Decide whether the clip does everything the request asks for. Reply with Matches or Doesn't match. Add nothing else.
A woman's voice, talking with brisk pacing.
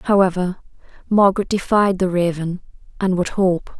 Doesn't match